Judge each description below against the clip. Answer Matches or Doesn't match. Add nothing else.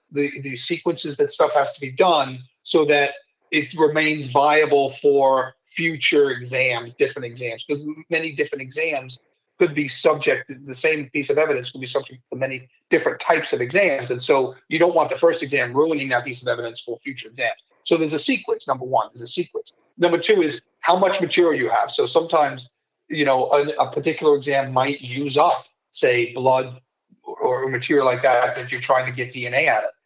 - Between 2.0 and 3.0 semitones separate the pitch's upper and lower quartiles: Doesn't match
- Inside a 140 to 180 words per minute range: Doesn't match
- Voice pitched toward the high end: Doesn't match